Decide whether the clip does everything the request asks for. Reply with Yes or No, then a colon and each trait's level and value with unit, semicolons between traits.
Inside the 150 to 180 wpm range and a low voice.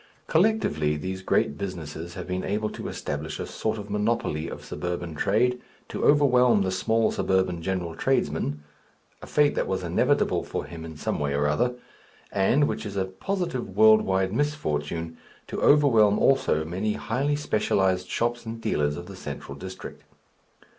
Yes: average, 160 wpm; very low, 95 Hz